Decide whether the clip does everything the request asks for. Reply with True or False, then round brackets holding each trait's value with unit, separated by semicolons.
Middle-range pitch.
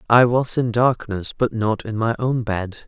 False (115 Hz)